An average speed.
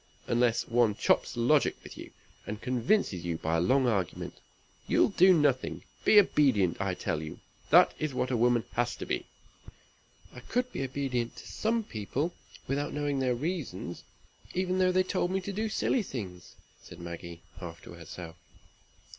Yes: average, 170 wpm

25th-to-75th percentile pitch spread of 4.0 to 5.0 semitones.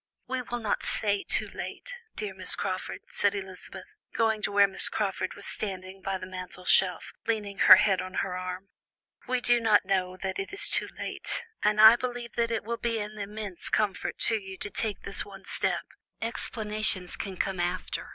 No: average, 2.9 semitones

